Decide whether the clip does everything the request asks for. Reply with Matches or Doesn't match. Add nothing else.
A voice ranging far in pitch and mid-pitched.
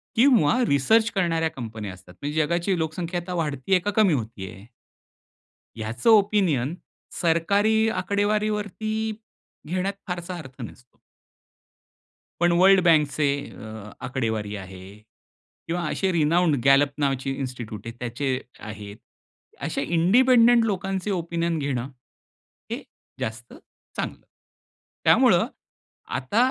Matches